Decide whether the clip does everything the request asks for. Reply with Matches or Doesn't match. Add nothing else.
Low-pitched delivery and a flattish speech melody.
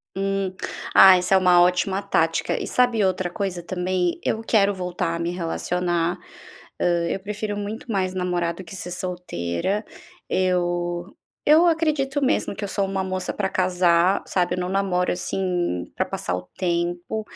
Doesn't match